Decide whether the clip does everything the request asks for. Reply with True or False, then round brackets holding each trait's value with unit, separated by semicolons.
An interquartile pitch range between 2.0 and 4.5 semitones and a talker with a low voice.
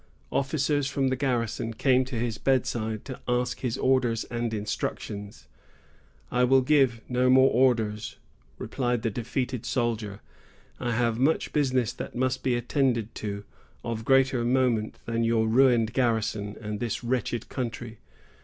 True (2.5 semitones; 120 Hz)